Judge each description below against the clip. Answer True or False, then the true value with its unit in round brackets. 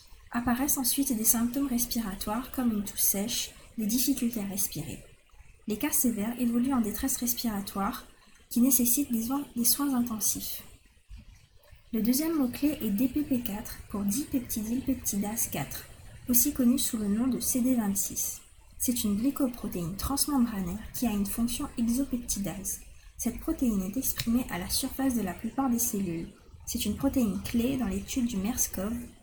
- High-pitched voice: True (235 Hz)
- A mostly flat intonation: False (3.9 semitones)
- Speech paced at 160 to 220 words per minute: False (145 wpm)